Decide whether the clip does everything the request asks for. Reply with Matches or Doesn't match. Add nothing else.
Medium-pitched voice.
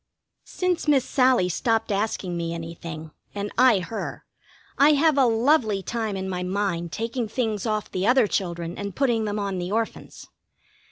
Doesn't match